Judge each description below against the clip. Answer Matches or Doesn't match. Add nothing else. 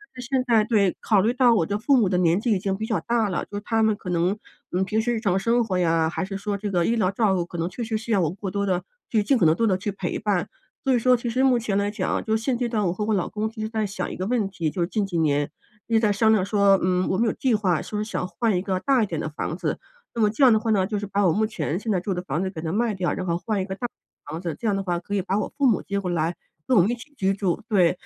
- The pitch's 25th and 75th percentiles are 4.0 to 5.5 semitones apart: Doesn't match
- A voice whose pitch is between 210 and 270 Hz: Doesn't match